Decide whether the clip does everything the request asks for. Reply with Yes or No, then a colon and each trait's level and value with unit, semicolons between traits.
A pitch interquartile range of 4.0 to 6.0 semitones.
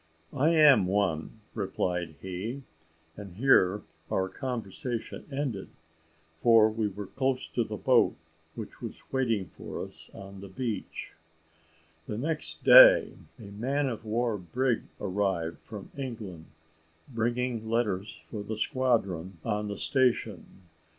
Yes: average, 4.6 semitones